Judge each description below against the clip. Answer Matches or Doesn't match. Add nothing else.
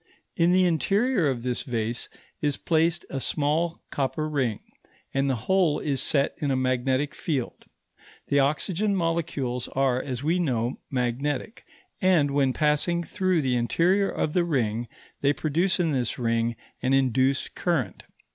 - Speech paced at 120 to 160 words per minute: Matches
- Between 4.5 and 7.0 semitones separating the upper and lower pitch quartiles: Matches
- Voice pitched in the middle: Matches